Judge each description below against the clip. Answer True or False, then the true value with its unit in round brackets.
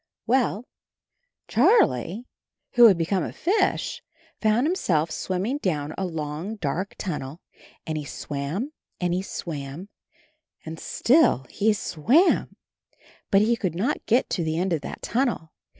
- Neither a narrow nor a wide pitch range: False (6.7 semitones)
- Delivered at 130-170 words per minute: True (135 wpm)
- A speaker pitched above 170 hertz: True (185 Hz)